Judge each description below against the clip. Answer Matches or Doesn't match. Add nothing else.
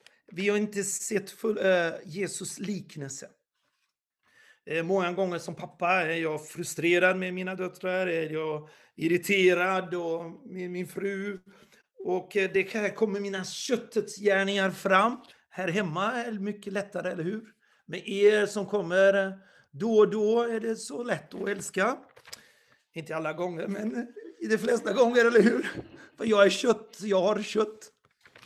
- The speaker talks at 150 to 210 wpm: Doesn't match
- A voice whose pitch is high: Matches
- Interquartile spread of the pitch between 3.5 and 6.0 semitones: Doesn't match